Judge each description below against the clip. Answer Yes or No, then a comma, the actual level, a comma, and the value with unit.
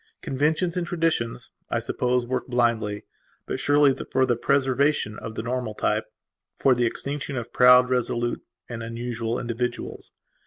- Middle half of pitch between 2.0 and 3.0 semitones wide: Yes, narrow, 2.6 semitones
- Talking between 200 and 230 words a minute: No, average, 145 wpm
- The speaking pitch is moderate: No, low, 125 Hz